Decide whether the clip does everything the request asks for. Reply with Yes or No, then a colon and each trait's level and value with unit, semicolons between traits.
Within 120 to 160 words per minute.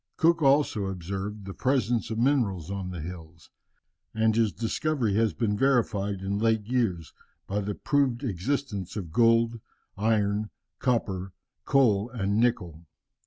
Yes: slow, 135 wpm